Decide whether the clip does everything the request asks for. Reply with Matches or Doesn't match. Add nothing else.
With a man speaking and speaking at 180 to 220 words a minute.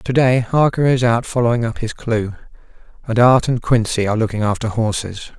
Matches